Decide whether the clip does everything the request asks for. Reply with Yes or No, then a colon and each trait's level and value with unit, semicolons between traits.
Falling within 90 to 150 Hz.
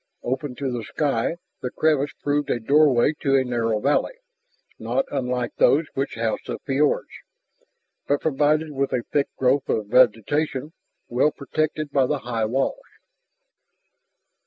Yes: low, 135 Hz